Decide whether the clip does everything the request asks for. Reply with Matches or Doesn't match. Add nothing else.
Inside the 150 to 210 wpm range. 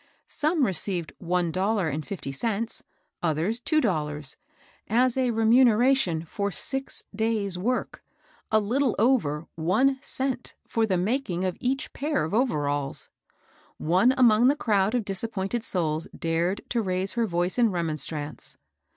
Doesn't match